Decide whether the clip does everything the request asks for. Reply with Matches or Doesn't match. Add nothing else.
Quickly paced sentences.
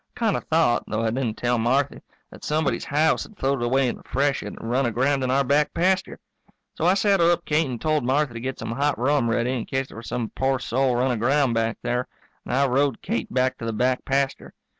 Matches